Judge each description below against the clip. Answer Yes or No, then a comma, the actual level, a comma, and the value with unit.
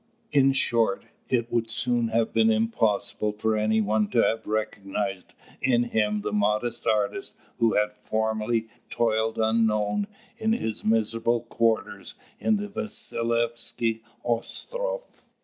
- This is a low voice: Yes, low, 115 Hz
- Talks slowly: Yes, slow, 125 wpm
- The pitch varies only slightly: Yes, narrow, 1.7 semitones